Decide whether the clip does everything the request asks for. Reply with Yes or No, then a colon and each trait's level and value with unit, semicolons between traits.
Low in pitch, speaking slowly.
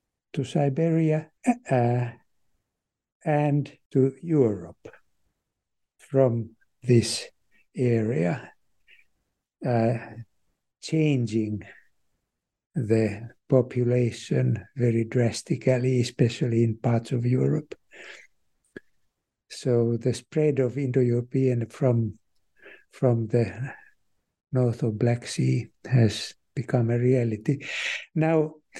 Yes: low, 125 Hz; slow, 75 wpm